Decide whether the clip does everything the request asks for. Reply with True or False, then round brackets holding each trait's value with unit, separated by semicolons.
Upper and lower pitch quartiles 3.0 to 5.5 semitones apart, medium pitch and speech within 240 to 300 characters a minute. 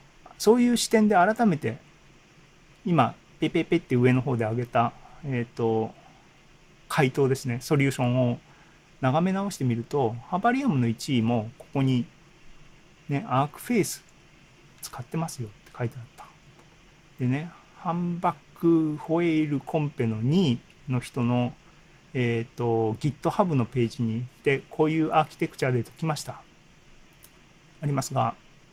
True (5.1 semitones; 145 Hz; 290 characters per minute)